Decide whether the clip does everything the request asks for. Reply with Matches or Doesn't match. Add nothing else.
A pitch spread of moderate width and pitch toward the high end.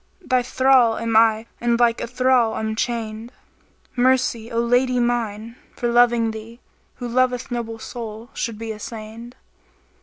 Doesn't match